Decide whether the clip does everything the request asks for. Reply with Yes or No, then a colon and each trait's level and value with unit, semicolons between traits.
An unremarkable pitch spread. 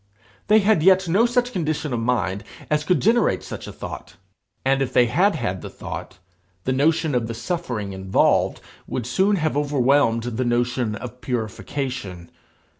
No: wide, 5.9 semitones